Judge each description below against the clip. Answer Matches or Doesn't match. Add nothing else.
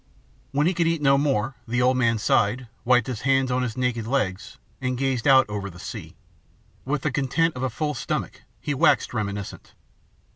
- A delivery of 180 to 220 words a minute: Matches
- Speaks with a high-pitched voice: Doesn't match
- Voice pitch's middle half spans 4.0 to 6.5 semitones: Doesn't match